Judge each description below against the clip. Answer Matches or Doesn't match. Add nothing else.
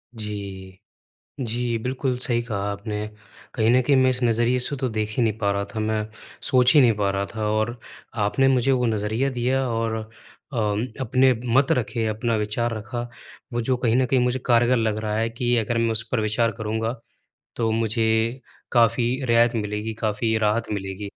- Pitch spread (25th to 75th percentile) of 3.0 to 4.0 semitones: Doesn't match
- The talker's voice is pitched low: Matches